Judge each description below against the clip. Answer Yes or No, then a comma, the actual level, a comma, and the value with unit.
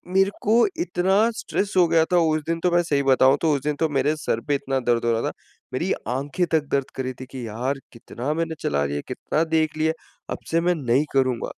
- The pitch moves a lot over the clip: No, average, 4.1 semitones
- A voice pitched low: No, medium, 145 Hz